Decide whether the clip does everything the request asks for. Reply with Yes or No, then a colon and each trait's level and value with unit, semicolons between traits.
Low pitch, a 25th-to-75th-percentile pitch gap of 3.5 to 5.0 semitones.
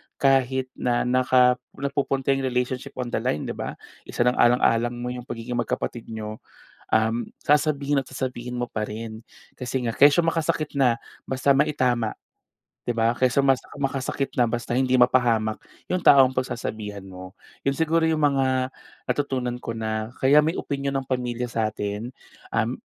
No: low, 125 Hz; narrow, 2.6 semitones